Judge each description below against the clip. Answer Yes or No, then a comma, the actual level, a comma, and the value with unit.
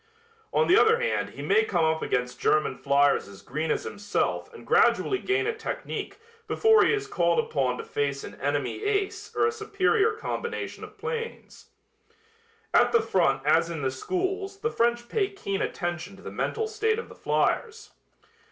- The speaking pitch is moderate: No, very high, 375 Hz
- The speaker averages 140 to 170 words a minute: No, average, 180 wpm